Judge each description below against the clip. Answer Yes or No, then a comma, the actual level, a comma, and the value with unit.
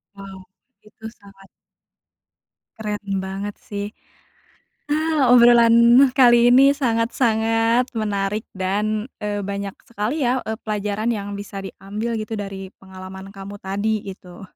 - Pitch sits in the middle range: No, high, 210 Hz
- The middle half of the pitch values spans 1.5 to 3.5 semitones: Yes, narrow, 2.5 semitones